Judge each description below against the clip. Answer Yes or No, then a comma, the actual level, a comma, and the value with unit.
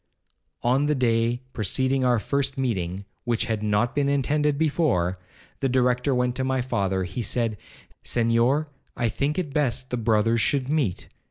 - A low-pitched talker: Yes, low, 125 Hz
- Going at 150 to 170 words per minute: Yes, average, 160 wpm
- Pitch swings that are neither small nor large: Yes, average, 3.4 semitones